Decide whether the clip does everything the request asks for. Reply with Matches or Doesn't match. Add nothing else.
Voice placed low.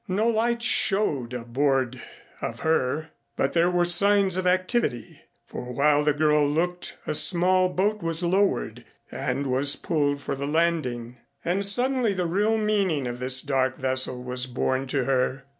Doesn't match